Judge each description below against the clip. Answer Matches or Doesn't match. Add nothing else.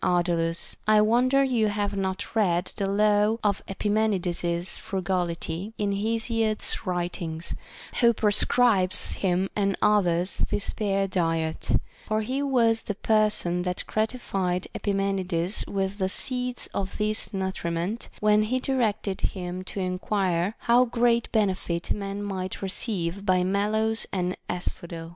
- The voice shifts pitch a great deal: Doesn't match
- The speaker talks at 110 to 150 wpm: Matches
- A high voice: Matches